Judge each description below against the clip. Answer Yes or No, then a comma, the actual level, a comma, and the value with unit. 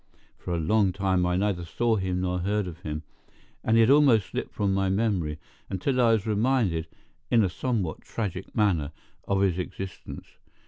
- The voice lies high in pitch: No, very low, 95 Hz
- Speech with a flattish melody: No, average, 3.7 semitones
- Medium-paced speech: Yes, average, 180 wpm